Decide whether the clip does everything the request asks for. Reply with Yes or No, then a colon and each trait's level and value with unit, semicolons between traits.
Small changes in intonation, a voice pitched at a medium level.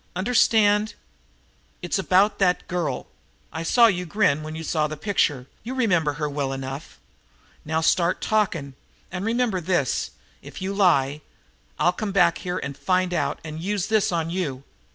No: average, 4.5 semitones; medium, 180 Hz